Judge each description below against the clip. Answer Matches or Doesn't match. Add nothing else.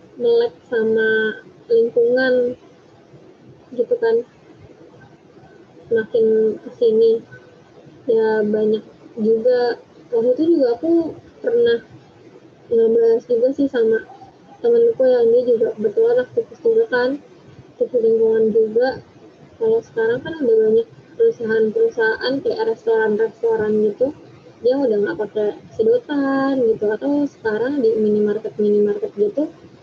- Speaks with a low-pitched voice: Doesn't match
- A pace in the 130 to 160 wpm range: Doesn't match